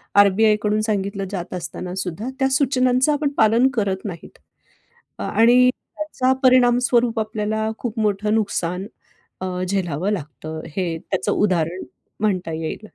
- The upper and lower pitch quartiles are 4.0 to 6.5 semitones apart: Yes, average, 4.3 semitones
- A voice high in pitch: Yes, high, 210 Hz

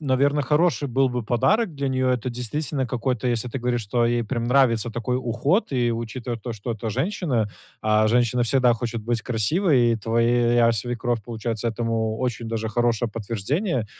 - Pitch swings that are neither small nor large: No, narrow, 2.2 semitones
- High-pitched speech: No, low, 120 Hz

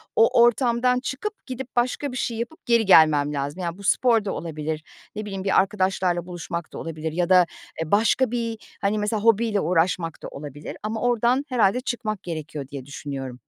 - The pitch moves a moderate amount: No, wide, 6.3 semitones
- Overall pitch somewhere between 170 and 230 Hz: Yes, high, 195 Hz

